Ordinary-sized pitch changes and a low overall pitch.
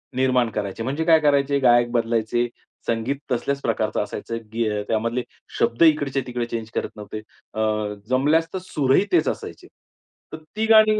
Yes: average, 4.1 semitones; low, 125 Hz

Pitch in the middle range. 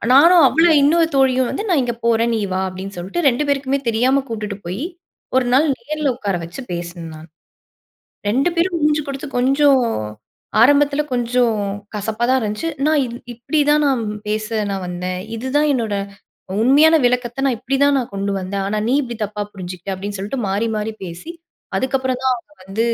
No: high, 245 Hz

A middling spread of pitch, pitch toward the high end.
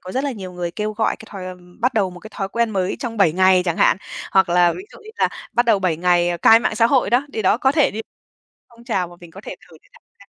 Yes: average, 4.6 semitones; high, 200 Hz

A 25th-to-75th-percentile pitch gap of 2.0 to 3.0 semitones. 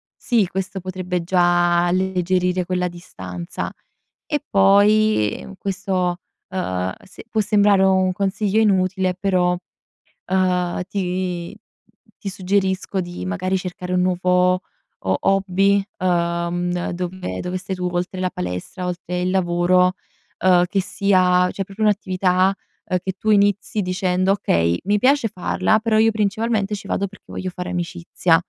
No: narrow, 1.6 semitones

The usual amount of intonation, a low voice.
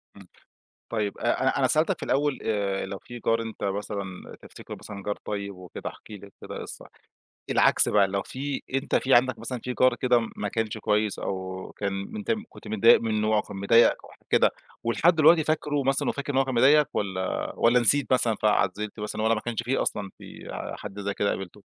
Yes: average, 4.2 semitones; low, 110 Hz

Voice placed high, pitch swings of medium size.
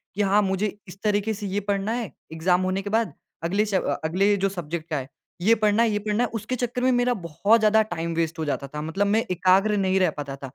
Yes: high, 200 Hz; average, 3.5 semitones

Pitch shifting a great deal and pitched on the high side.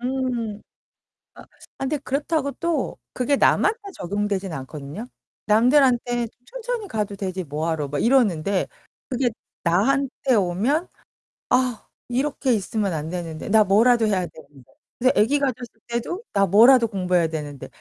Yes: wide, 6.4 semitones; high, 225 Hz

